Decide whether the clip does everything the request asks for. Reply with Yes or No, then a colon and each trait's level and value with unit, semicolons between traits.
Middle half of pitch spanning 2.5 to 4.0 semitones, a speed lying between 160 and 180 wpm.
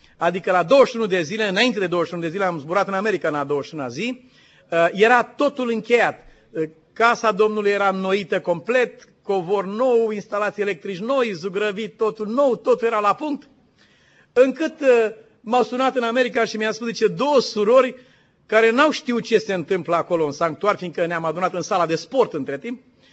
No: average, 4.6 semitones; fast, 170 wpm